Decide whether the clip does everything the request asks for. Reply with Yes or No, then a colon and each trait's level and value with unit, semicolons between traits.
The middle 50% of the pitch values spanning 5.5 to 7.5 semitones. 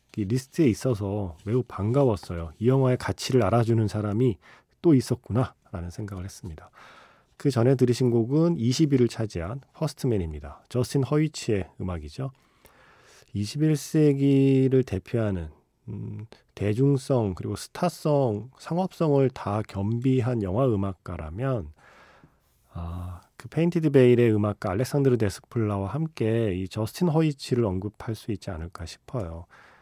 No: average, 5.1 semitones